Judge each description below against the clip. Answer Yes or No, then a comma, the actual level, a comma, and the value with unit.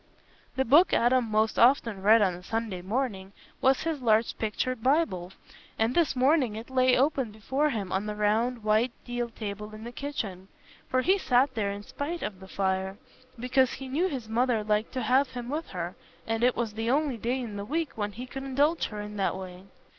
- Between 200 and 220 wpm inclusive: Yes, fast, 205 wpm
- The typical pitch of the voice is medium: No, high, 230 Hz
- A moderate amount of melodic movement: Yes, average, 4.0 semitones